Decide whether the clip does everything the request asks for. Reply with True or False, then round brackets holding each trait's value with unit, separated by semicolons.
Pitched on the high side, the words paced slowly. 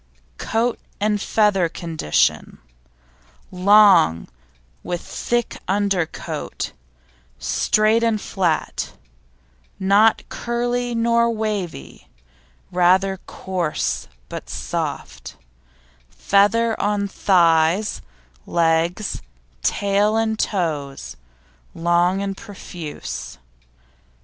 True (195 Hz; 75 wpm)